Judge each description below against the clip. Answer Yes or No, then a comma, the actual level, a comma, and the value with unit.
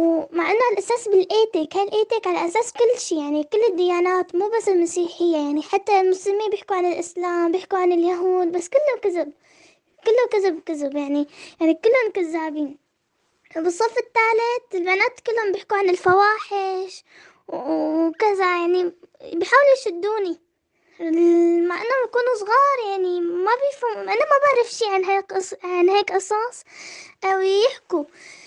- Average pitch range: Yes, average, 4.0 semitones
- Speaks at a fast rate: Yes, fast, 140 wpm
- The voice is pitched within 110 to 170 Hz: No, very high, 375 Hz